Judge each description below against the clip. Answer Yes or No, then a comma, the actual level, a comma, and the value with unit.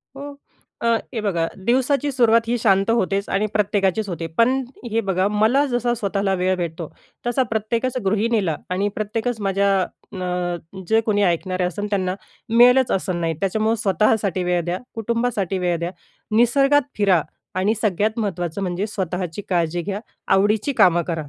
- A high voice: Yes, high, 205 Hz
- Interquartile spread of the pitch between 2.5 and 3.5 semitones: No, average, 3.9 semitones